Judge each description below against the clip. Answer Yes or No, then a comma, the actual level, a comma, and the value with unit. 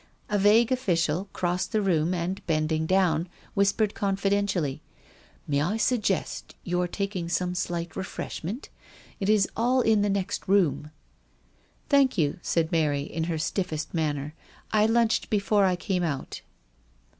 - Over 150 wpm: No, average, 145 wpm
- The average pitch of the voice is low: No, medium, 185 Hz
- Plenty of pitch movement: No, average, 3.9 semitones